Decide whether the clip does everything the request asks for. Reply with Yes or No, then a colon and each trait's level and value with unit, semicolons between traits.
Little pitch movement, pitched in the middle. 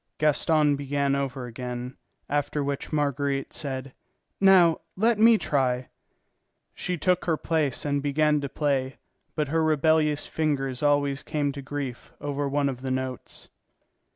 Yes: narrow, 2.1 semitones; medium, 145 Hz